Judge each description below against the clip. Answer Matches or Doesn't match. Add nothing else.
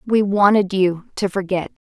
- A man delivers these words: Doesn't match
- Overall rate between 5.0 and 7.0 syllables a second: Doesn't match